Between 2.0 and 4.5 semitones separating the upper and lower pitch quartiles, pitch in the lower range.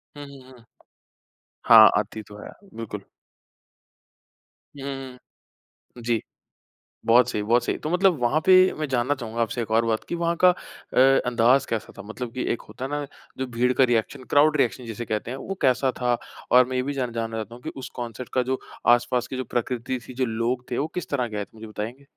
Yes: narrow, 2.5 semitones; low, 125 Hz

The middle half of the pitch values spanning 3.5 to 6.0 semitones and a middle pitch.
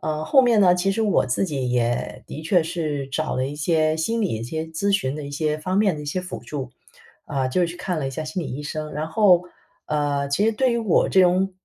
Yes: average, 4.4 semitones; medium, 160 Hz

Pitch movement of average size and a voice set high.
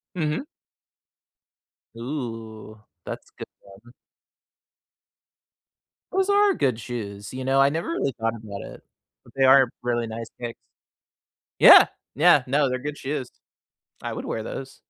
No: average, 4.1 semitones; low, 130 Hz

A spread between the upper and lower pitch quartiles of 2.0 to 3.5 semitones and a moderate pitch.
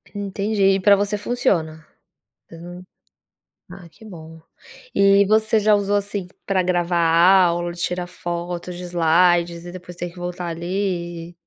Yes: narrow, 2.5 semitones; medium, 180 Hz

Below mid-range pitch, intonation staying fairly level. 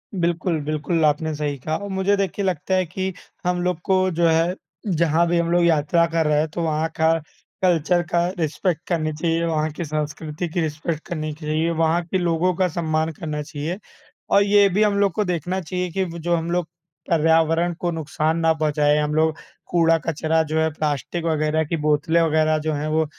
No: medium, 165 Hz; narrow, 2.1 semitones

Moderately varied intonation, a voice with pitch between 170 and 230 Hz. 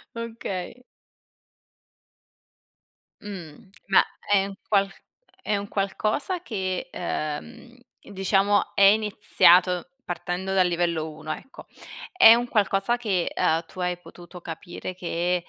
Yes: average, 3.0 semitones; high, 190 Hz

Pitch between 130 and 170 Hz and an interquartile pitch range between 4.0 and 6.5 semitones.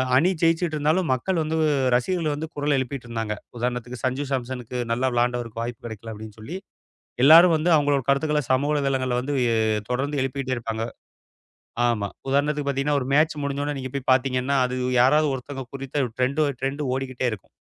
No: low, 135 Hz; average, 3.1 semitones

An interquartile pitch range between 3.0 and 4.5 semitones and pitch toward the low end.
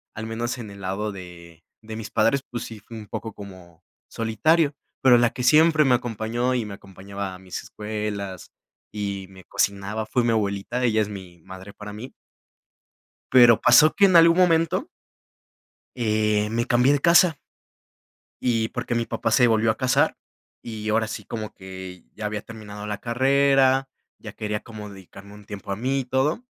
Yes: average, 3.7 semitones; low, 110 Hz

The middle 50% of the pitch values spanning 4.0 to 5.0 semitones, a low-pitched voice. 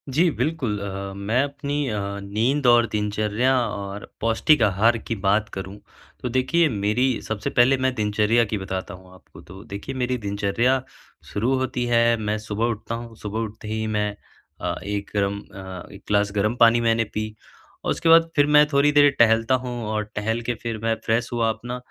No: average, 3.2 semitones; low, 115 Hz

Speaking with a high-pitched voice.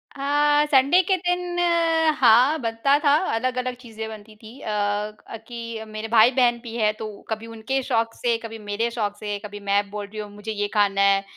Yes: high, 230 Hz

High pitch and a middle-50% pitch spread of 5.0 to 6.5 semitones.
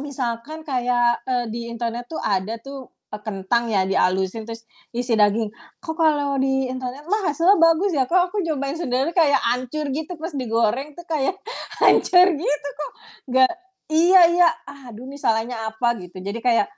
Yes: very high, 260 Hz; average, 5.3 semitones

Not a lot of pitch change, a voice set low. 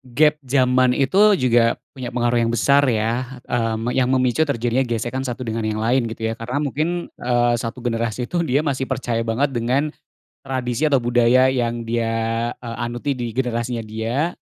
Yes: narrow, 2.2 semitones; low, 120 Hz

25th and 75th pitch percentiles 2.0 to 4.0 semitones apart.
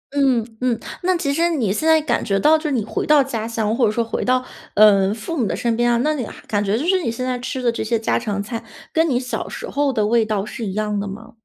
No: average, 4.4 semitones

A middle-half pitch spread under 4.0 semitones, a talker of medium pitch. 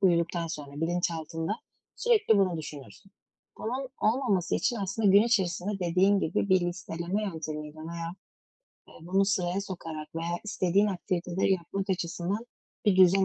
Yes: average, 2.9 semitones; medium, 180 Hz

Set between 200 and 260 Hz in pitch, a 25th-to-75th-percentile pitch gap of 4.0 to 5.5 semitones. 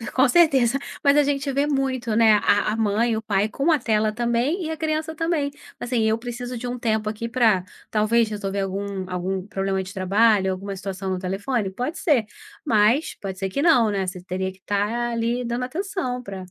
Yes: high, 225 Hz; average, 4.4 semitones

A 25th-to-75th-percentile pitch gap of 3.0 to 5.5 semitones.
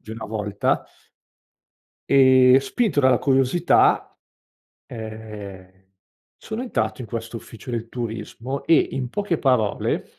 Yes: average, 3.4 semitones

